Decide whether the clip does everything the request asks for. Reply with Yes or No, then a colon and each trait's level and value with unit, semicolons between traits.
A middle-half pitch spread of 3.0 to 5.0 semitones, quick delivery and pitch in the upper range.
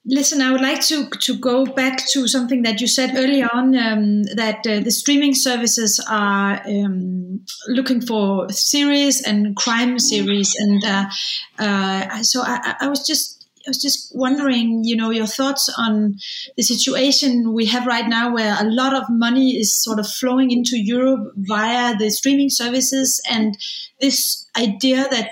No: average, 3.6 semitones; average, 170 wpm; high, 240 Hz